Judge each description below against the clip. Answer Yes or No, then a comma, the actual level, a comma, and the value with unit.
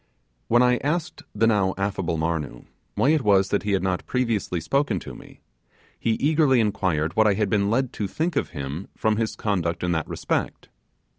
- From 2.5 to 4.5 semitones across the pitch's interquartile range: No, average, 5.1 semitones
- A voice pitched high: No, low, 105 Hz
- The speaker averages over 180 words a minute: Yes, average, 195 wpm